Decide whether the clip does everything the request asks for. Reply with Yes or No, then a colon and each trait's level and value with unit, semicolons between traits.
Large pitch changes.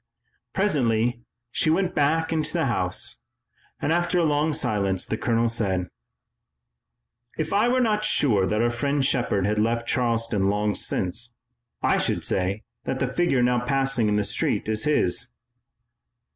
Yes: wide, 5.9 semitones